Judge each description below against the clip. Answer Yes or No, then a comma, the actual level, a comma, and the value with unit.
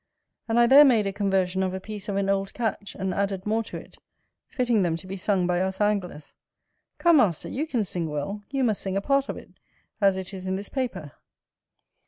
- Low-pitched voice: No, high, 195 Hz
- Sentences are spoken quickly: Yes, fast, 225 wpm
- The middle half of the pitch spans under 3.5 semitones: Yes, average, 3.1 semitones